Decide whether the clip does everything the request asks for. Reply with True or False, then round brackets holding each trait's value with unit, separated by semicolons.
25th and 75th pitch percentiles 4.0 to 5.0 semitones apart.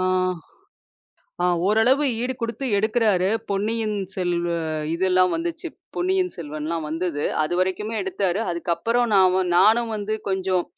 True (4.3 semitones)